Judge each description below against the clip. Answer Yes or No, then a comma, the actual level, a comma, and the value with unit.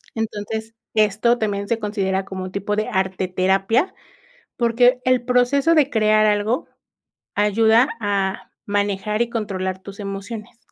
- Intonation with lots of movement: No, average, 2.8 semitones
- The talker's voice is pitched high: Yes, high, 210 Hz